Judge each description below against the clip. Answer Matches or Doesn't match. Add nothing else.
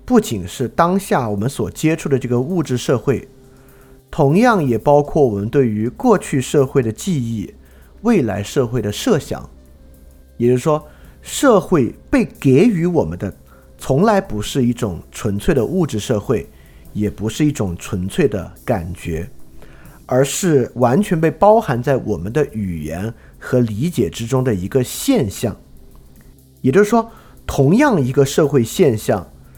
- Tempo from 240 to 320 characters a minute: Doesn't match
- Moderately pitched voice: Doesn't match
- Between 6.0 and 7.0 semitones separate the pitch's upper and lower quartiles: Doesn't match